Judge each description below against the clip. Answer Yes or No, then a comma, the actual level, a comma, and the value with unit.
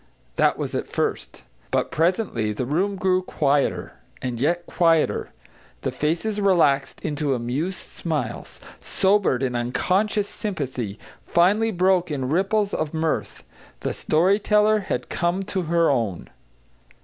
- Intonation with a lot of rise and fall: Yes, wide, 5.7 semitones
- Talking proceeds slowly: Yes, slow, 130 wpm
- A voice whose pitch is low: No, medium, 170 Hz